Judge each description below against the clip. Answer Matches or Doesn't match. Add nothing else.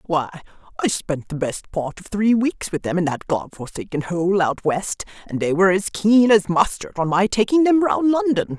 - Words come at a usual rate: Doesn't match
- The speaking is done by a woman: Matches